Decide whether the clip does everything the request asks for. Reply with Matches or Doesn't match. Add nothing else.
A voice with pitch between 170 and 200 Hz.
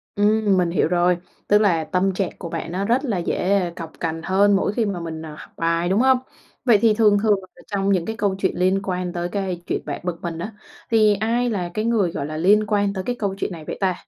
Matches